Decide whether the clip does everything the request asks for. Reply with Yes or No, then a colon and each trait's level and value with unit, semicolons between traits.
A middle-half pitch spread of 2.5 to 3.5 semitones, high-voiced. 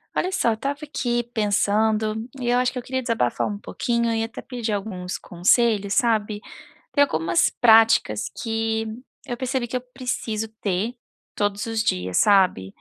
Yes: average, 3.0 semitones; high, 225 Hz